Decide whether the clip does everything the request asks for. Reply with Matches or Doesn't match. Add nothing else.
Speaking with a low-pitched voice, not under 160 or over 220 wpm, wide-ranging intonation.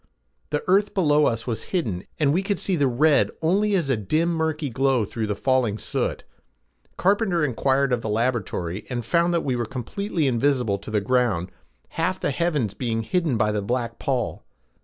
Matches